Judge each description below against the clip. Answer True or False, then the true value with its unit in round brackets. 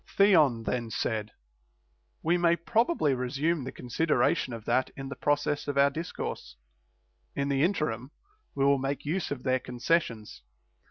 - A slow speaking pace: False (160 wpm)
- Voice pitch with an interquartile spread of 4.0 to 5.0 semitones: True (4.4 semitones)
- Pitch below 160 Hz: True (140 Hz)